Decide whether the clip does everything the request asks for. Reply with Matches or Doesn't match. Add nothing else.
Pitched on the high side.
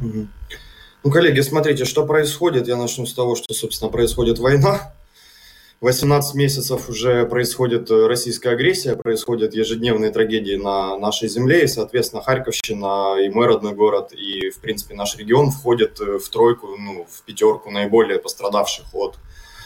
Doesn't match